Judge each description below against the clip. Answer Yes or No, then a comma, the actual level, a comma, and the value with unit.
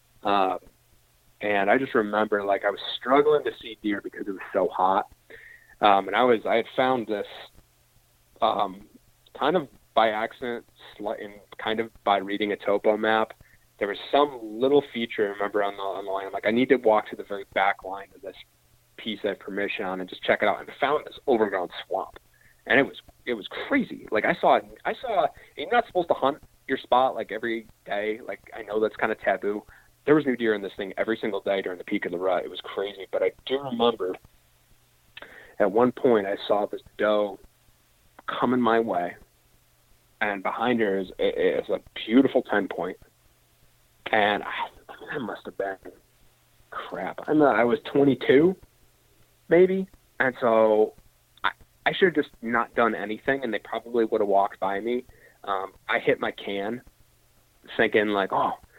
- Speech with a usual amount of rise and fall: Yes, average, 4.1 semitones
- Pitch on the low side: Yes, low, 115 Hz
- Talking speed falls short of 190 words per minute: No, average, 195 wpm